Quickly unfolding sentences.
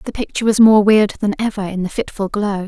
Yes: fast, 245 wpm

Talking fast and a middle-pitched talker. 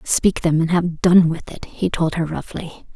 Yes: fast, 225 wpm; medium, 165 Hz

